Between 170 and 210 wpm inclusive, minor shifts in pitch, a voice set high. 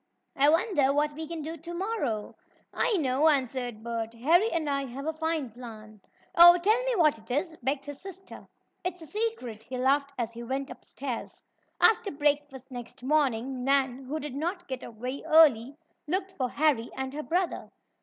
No: average, 185 wpm; average, 4.5 semitones; very high, 280 Hz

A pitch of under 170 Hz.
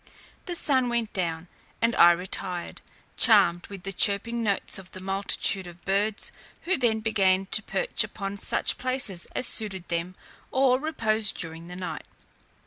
No: high, 200 Hz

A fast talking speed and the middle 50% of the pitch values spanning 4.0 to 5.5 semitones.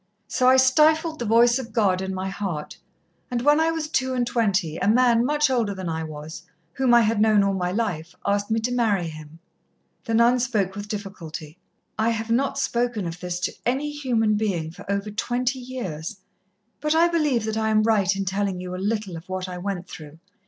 Yes: fast, 210 wpm; average, 4.8 semitones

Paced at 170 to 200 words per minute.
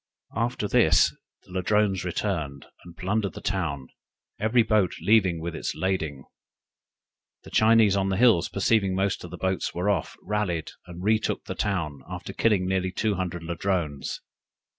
No: average, 155 wpm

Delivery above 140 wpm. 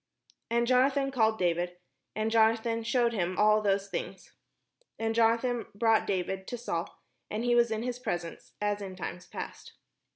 Yes: average, 160 wpm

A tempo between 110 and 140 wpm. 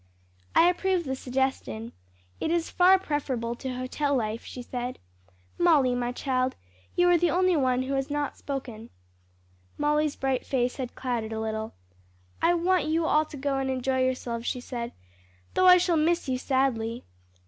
No: average, 170 wpm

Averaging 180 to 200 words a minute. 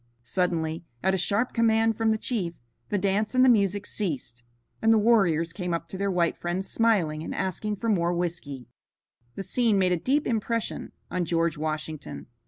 Yes: average, 185 wpm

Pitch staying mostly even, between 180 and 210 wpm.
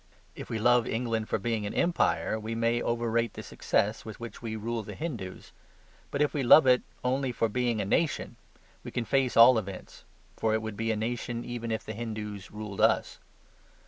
Yes: narrow, 1.9 semitones; average, 200 wpm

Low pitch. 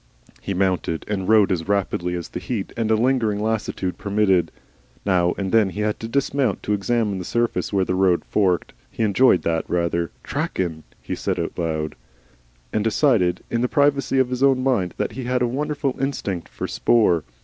Yes: low, 105 Hz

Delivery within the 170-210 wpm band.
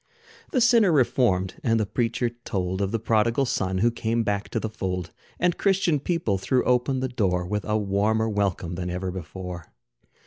Yes: average, 180 wpm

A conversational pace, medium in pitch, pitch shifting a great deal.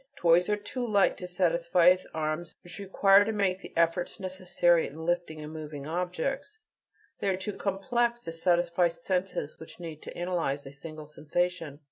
No: average, 165 wpm; medium, 175 Hz; average, 2.9 semitones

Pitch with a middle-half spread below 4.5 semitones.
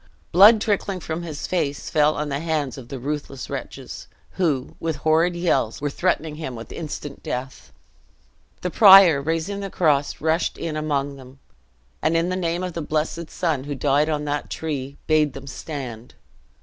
Yes: average, 3.1 semitones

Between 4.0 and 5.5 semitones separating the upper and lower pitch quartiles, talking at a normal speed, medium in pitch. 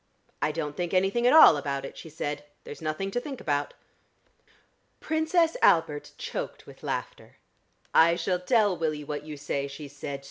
Yes: average, 5.0 semitones; average, 170 wpm; medium, 160 Hz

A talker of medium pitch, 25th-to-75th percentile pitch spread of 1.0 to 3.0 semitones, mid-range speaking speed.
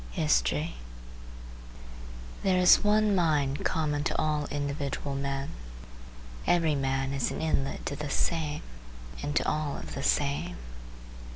No: medium, 145 Hz; narrow, 2.4 semitones; slow, 125 wpm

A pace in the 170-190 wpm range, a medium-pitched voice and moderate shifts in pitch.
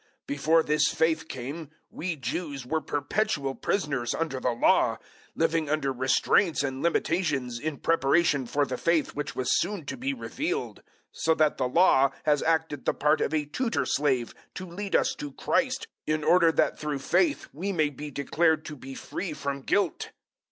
Yes: average, 180 wpm; medium, 155 Hz; average, 3.5 semitones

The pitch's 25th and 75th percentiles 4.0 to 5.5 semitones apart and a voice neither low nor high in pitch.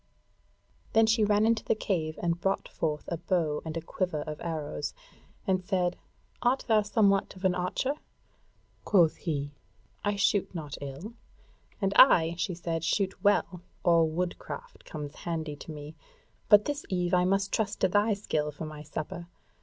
Yes: average, 4.4 semitones; medium, 180 Hz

